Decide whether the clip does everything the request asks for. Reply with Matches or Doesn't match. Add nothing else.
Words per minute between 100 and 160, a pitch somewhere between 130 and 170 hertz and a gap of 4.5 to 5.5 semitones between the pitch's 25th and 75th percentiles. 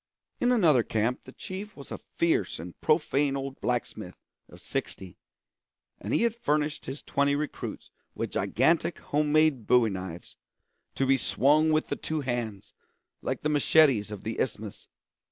Matches